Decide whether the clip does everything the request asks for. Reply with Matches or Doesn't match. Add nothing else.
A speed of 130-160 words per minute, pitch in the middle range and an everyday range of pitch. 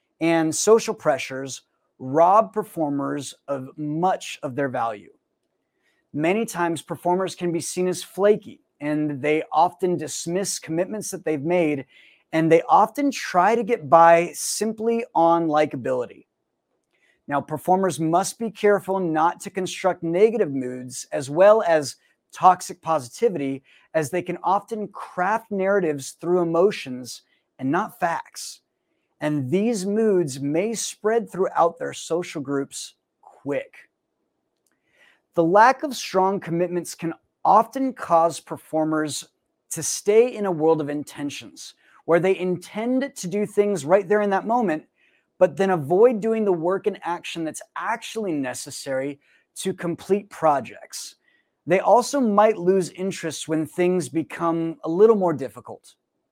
Matches